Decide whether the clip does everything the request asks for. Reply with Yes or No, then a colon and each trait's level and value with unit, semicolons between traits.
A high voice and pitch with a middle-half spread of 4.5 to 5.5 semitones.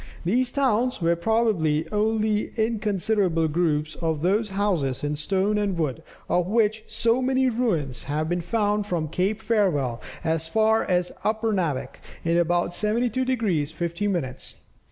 Yes: high, 195 Hz; average, 5.1 semitones